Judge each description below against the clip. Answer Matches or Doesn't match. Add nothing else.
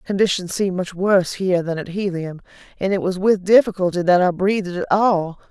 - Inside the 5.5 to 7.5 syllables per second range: Matches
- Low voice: Doesn't match